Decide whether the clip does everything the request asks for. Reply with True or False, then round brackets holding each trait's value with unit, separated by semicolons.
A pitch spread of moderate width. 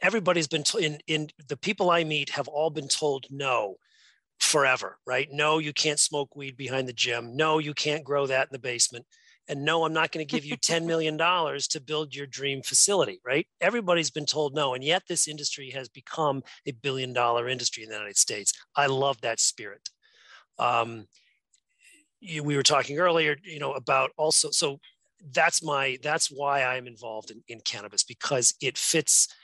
True (3.2 semitones)